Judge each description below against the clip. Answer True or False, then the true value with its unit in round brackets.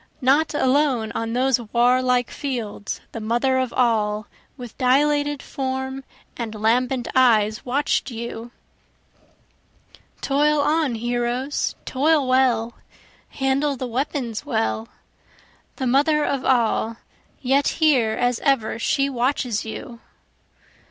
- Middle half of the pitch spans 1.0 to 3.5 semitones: True (2.9 semitones)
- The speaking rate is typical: False (110 wpm)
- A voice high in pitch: True (255 Hz)